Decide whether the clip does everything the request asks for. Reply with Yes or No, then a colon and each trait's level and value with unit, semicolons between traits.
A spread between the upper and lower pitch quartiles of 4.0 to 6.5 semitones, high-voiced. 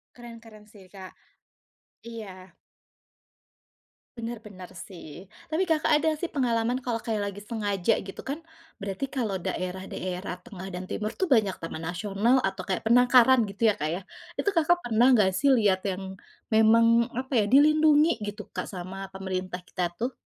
Yes: average, 4.3 semitones; high, 215 Hz